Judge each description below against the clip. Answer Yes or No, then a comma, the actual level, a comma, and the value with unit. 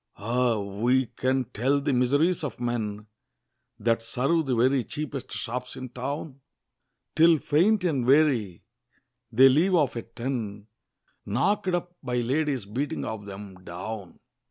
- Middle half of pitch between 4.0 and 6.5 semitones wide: Yes, average, 4.3 semitones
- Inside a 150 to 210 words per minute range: No, slow, 135 wpm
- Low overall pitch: Yes, low, 125 Hz